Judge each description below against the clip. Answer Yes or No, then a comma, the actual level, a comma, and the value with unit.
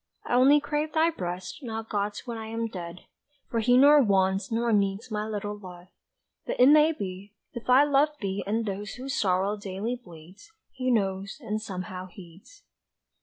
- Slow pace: No, average, 175 wpm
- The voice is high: Yes, high, 210 Hz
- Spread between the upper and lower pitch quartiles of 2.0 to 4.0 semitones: No, average, 4.6 semitones